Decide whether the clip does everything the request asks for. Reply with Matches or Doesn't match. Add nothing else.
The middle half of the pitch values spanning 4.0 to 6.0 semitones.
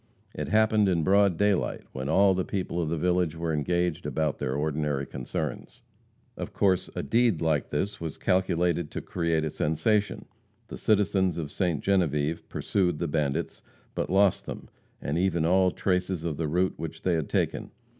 Doesn't match